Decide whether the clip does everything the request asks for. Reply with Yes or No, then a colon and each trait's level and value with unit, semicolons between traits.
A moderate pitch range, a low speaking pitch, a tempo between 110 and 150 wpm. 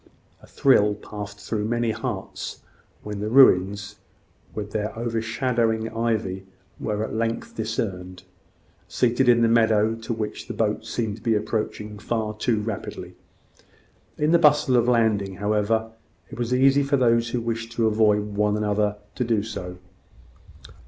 No: narrow, 2.0 semitones; low, 110 Hz; average, 145 wpm